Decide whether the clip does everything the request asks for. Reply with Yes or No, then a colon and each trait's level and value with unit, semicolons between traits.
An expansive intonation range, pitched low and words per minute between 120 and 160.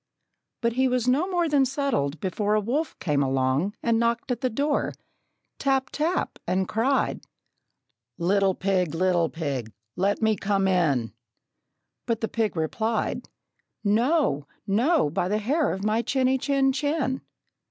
No: wide, 6.5 semitones; high, 220 Hz; average, 145 wpm